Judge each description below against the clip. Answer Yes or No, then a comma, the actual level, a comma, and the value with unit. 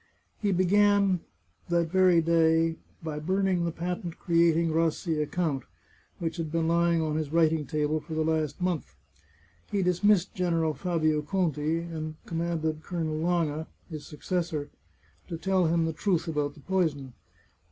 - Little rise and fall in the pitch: Yes, narrow, 2.1 semitones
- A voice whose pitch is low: No, medium, 165 Hz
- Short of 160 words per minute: Yes, average, 150 wpm